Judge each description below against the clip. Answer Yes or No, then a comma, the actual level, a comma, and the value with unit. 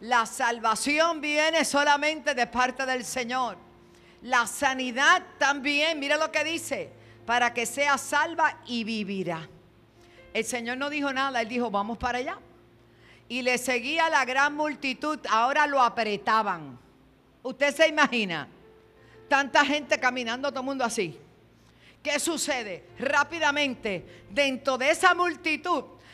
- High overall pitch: Yes, very high, 260 Hz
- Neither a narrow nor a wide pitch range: Yes, average, 4.3 semitones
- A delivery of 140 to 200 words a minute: No, average, 130 wpm